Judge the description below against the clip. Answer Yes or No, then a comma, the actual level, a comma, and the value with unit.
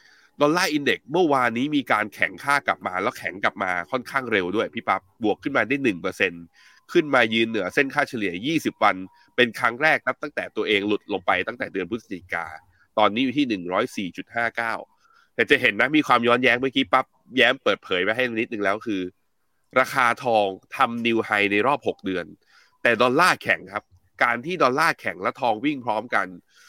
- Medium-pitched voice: No, low, 125 Hz